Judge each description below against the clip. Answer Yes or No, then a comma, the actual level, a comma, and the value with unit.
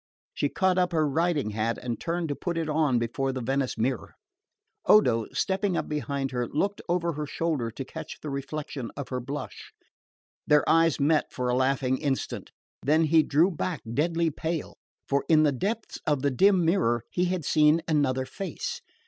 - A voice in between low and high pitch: Yes, medium, 150 Hz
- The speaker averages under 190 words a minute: Yes, average, 180 wpm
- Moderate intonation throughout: Yes, average, 4.1 semitones